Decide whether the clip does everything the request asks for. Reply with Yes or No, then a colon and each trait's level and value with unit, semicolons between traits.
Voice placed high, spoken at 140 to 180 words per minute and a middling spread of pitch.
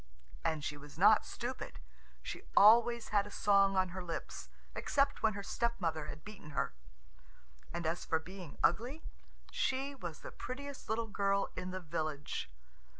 No: high, 195 Hz; average, 155 wpm; wide, 5.9 semitones